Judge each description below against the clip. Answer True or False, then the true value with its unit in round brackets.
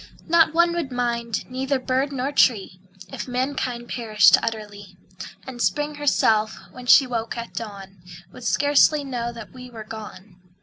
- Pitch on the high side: True (245 Hz)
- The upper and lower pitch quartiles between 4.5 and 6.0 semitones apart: False (3.7 semitones)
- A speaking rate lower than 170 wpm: True (150 wpm)